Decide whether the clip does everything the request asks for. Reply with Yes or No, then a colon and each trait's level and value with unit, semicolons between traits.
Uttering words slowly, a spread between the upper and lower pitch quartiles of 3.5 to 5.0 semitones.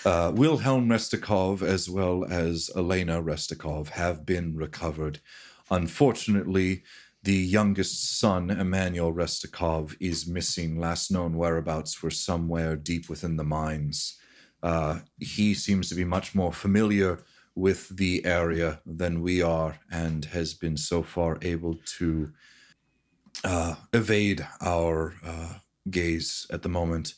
No: slow, 125 wpm; narrow, 2.4 semitones